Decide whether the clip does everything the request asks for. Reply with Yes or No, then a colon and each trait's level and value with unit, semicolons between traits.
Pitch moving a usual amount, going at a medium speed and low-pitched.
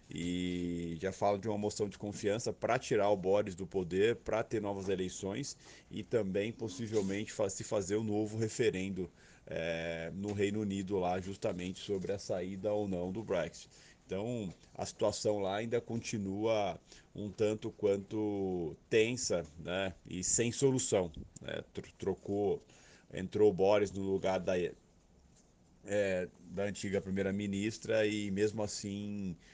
No: narrow, 2.1 semitones; average, 140 wpm; low, 100 Hz